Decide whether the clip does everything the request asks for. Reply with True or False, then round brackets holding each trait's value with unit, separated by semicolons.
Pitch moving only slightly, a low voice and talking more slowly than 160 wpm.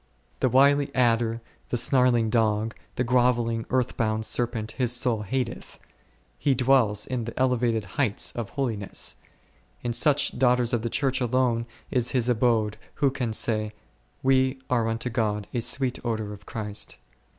True (2.3 semitones; 120 Hz; 150 wpm)